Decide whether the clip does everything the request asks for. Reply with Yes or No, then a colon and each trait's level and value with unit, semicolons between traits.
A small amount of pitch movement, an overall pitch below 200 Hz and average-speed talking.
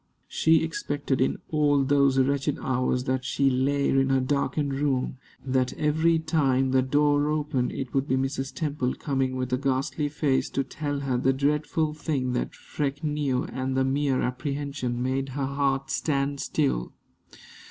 Yes: narrow, 1.9 semitones; low, 135 Hz; average, 165 wpm